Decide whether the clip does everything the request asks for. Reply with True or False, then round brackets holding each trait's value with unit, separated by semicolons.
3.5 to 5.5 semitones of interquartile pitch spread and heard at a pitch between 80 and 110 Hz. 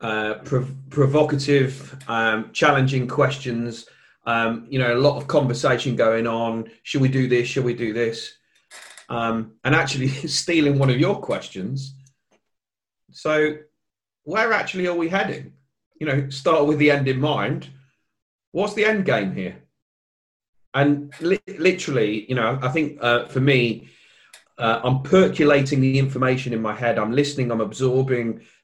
False (3.9 semitones; 135 Hz)